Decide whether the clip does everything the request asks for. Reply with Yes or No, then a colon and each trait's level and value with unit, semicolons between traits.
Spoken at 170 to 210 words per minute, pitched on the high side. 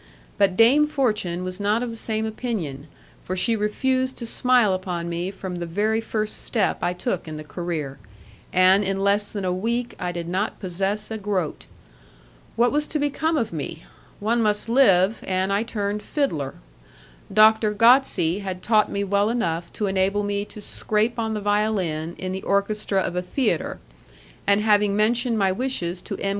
Yes: average, 180 wpm; high, 205 Hz